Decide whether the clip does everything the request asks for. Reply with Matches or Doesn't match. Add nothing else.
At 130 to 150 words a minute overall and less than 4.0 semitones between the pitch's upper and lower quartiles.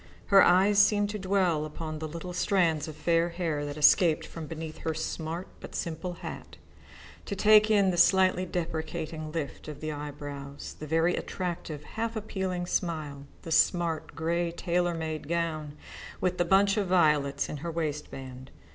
Doesn't match